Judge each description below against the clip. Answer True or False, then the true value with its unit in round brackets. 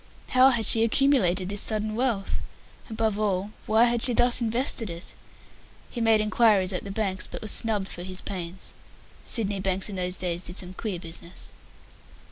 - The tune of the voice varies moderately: True (3.4 semitones)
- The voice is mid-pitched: False (210 Hz)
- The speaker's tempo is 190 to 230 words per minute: False (175 wpm)